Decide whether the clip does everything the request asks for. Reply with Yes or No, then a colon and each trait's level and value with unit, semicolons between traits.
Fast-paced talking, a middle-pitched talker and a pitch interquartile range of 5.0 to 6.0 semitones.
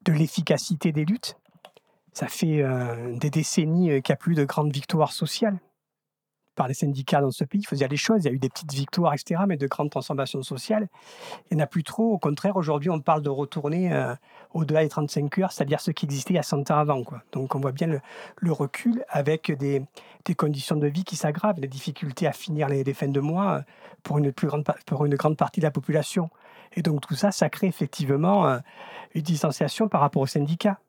No: fast, 230 wpm; medium, 155 Hz; average, 3.7 semitones